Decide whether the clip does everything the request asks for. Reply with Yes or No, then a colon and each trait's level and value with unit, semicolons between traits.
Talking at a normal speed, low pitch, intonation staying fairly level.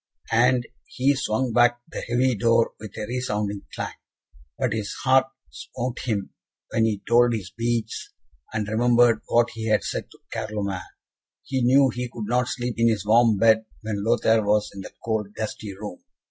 Yes: average, 175 wpm; low, 115 Hz; narrow, 2.3 semitones